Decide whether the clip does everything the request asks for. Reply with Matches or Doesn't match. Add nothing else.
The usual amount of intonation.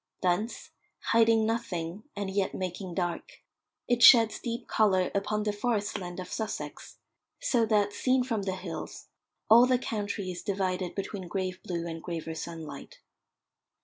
Matches